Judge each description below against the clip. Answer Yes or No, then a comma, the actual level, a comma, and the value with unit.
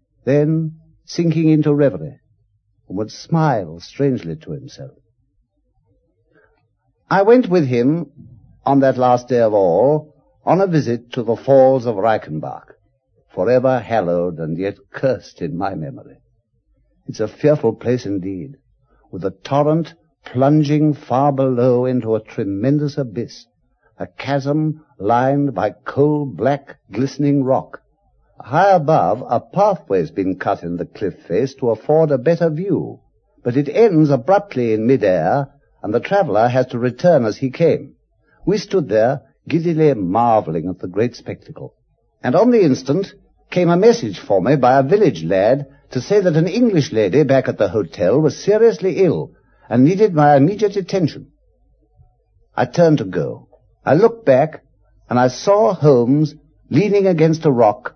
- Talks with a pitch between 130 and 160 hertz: Yes, medium, 140 Hz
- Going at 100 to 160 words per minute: Yes, average, 150 wpm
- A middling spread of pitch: Yes, average, 4.7 semitones